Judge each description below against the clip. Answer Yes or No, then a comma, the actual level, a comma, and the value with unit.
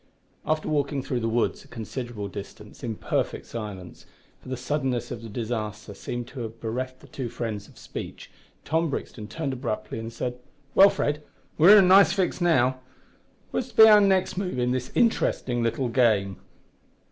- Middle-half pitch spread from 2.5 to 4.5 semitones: No, average, 5.2 semitones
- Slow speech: No, average, 180 wpm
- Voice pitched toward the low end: Yes, low, 125 Hz